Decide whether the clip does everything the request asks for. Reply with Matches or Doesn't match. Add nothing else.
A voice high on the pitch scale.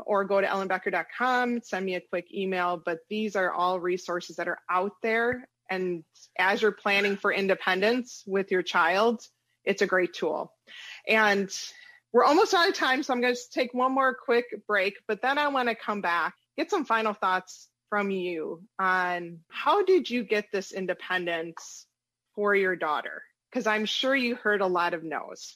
Matches